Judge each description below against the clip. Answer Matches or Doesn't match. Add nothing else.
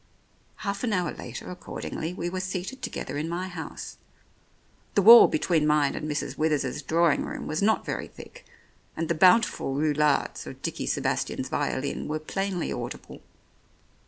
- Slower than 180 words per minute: Matches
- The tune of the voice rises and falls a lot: Doesn't match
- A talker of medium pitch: Matches